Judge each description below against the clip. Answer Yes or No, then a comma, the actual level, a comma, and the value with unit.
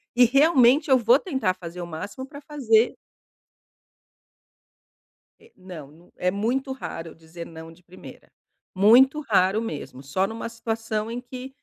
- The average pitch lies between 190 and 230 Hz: Yes, high, 225 Hz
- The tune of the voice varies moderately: No, wide, 6.6 semitones